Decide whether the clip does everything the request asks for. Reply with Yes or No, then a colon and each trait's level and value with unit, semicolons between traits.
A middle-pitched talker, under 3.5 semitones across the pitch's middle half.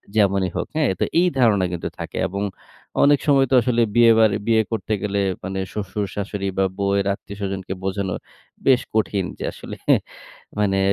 No: low, 100 Hz; narrow, 2.6 semitones